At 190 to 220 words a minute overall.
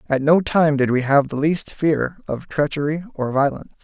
Yes: fast, 205 wpm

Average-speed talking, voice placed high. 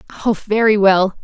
Yes: average, 145 wpm; high, 205 Hz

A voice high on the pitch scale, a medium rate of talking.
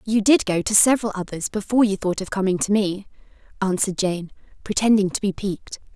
Yes: high, 200 Hz; average, 190 wpm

